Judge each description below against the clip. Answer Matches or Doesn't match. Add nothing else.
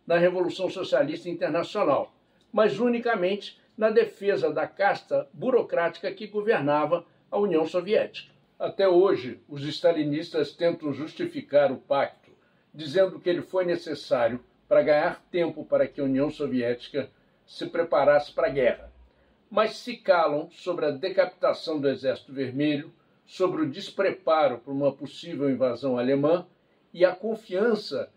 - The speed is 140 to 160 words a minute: Doesn't match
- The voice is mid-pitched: Matches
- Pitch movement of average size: Doesn't match